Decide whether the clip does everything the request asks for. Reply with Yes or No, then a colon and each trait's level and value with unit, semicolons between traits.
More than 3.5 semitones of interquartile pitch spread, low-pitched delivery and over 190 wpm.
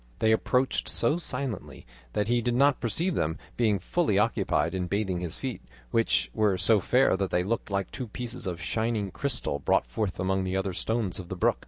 Yes: average, 4.3 semitones; low, 105 Hz; average, 200 wpm